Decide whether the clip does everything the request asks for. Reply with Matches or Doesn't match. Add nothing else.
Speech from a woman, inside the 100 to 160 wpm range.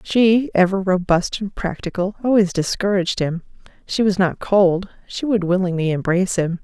Matches